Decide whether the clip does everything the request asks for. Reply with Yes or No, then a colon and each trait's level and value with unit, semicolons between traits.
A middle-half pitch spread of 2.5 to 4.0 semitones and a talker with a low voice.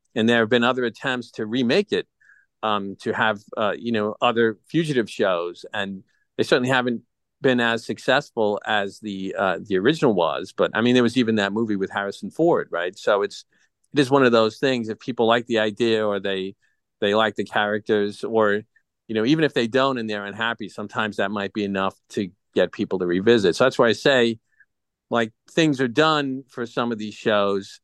Yes: average, 2.8 semitones; low, 110 Hz